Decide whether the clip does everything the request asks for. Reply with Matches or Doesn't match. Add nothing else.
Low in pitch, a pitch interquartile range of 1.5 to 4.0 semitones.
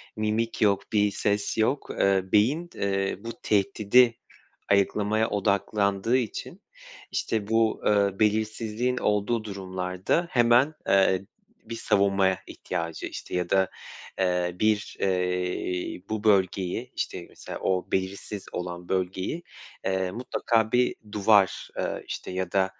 Matches